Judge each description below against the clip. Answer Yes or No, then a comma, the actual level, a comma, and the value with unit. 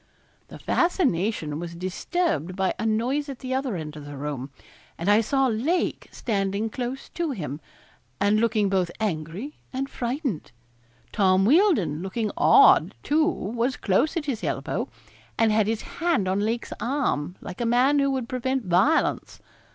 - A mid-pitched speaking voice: No, high, 220 Hz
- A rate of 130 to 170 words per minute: Yes, average, 160 wpm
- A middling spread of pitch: No, wide, 6.4 semitones